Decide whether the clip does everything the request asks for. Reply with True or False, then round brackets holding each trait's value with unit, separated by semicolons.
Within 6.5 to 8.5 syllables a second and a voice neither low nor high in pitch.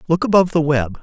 True (6.9 syllables/s; 160 Hz)